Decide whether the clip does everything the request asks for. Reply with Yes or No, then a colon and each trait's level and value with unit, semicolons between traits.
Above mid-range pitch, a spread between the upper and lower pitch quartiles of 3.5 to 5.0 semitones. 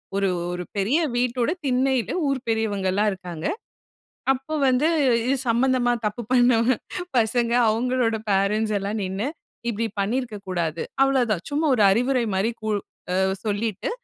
Yes: high, 230 Hz; average, 3.8 semitones